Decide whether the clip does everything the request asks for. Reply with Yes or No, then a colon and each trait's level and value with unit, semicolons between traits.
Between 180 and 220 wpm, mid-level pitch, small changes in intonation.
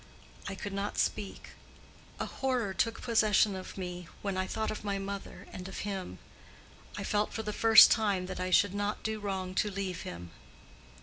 No: average, 185 wpm; high, 200 Hz; narrow, 2.1 semitones